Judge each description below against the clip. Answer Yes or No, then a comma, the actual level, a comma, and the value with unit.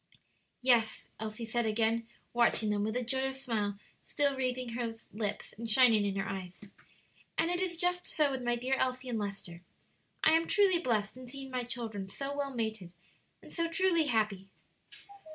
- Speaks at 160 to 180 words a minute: Yes, average, 175 wpm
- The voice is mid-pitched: No, high, 240 Hz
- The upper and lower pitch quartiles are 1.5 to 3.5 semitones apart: No, average, 3.9 semitones